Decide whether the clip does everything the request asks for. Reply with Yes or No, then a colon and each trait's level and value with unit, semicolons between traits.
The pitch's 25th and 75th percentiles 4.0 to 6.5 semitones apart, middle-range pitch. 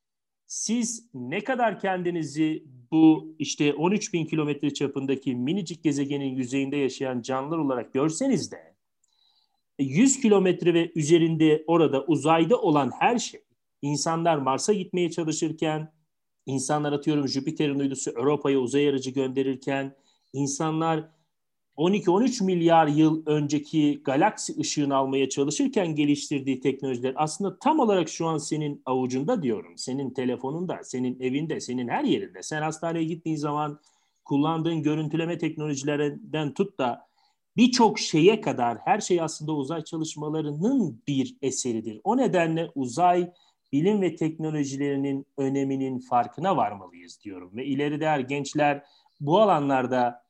No: average, 3.5 semitones; medium, 150 Hz